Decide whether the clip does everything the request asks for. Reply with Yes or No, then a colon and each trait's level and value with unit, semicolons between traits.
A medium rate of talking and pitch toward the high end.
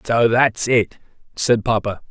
No: average, 145 wpm; low, 115 Hz